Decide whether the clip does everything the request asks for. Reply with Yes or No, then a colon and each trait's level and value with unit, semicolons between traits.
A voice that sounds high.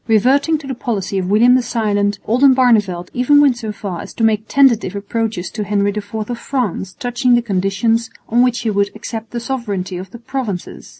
Yes: high, 225 Hz